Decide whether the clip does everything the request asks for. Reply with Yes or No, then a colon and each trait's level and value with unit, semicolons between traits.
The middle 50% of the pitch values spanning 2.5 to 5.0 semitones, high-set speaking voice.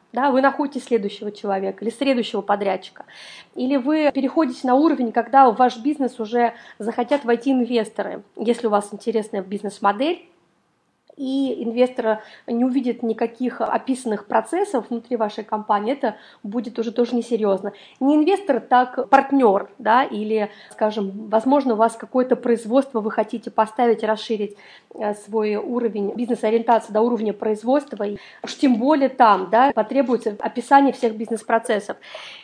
Yes: average, 2.9 semitones; high, 235 Hz